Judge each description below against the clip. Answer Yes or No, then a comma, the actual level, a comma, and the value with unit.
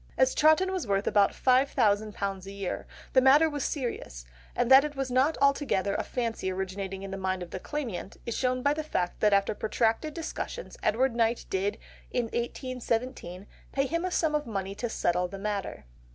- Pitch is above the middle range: Yes, high, 235 Hz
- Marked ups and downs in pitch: Yes, wide, 5.7 semitones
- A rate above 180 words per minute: Yes, average, 190 wpm